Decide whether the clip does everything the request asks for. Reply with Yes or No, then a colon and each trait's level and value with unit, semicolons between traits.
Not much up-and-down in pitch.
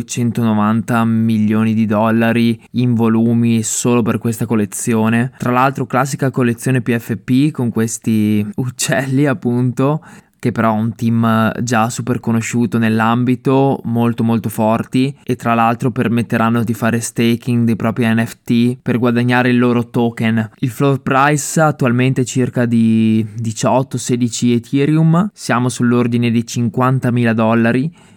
Yes: narrow, 1.9 semitones